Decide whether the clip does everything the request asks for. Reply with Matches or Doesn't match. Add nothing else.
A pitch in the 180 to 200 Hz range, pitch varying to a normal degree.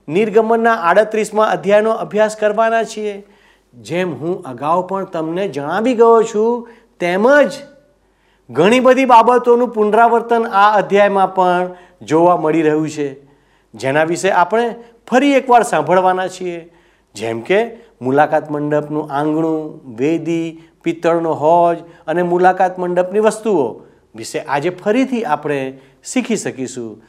Doesn't match